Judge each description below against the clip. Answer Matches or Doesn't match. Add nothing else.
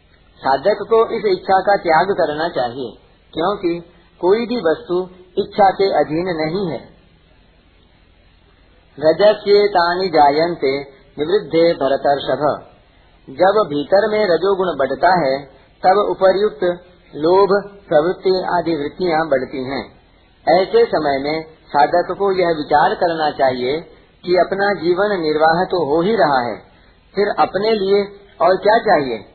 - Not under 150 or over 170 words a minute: Doesn't match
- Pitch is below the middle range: Doesn't match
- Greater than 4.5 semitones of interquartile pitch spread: Matches